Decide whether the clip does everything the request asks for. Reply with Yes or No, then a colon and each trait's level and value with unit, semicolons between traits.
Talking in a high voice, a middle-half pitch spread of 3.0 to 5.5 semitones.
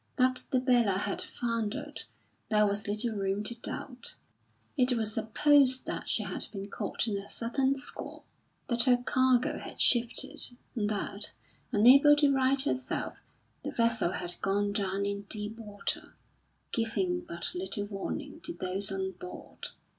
Yes: high, 225 Hz; average, 4.2 semitones